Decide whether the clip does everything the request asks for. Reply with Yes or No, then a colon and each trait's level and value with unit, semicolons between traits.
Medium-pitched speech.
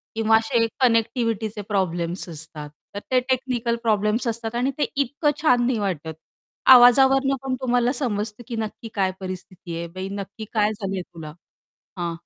No: high, 220 Hz